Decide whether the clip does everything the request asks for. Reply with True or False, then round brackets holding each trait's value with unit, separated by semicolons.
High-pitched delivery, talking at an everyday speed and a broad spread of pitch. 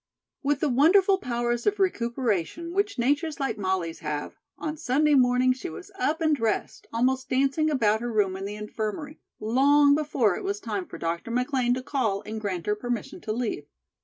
True (255 Hz; 185 wpm; 5.7 semitones)